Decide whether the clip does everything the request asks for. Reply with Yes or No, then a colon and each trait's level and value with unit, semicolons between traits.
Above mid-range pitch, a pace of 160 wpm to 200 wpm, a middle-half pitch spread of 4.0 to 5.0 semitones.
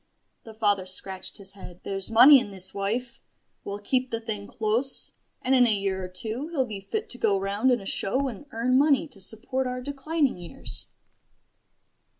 Yes: high, 225 Hz; average, 185 wpm; average, 4.7 semitones